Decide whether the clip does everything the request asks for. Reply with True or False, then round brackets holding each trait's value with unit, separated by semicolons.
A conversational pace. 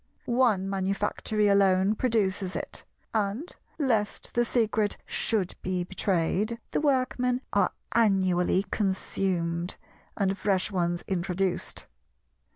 False (100 wpm)